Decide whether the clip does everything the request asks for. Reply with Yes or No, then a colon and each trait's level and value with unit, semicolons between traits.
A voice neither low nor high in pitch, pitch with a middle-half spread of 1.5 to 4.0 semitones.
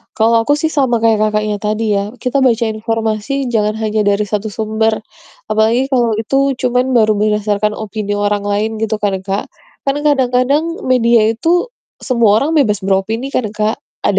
No: high, 220 Hz; average, 3.1 semitones